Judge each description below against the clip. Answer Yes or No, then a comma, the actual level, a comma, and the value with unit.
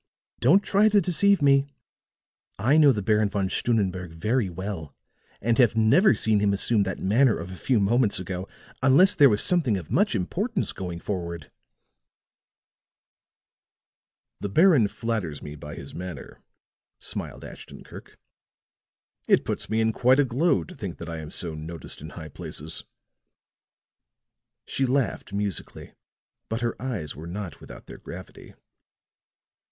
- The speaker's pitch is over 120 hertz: No, low, 105 Hz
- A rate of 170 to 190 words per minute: No, average, 145 wpm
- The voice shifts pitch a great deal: Yes, wide, 6.7 semitones